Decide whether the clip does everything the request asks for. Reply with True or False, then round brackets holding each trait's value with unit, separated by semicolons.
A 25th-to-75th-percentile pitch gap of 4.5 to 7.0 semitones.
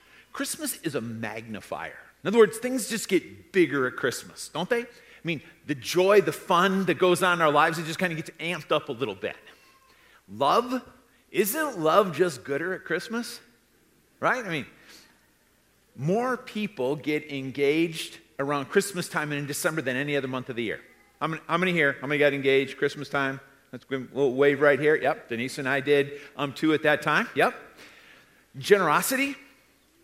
True (5.3 semitones)